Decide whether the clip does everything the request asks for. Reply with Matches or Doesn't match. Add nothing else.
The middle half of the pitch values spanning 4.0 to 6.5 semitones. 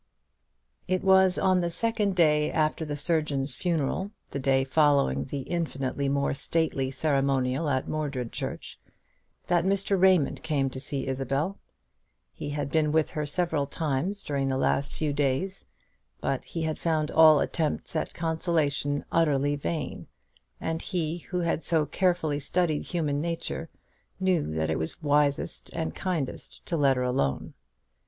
Doesn't match